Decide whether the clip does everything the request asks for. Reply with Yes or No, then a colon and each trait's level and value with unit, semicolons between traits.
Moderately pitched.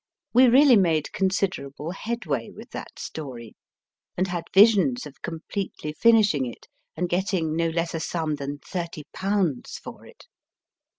Yes: medium, 170 Hz